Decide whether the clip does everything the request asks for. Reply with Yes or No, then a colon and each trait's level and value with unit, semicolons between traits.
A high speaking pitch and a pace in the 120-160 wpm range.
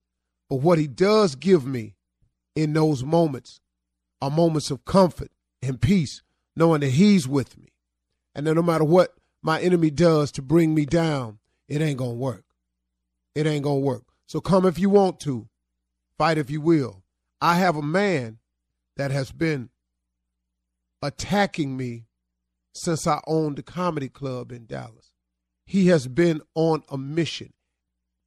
No: medium, 140 Hz; average, 155 wpm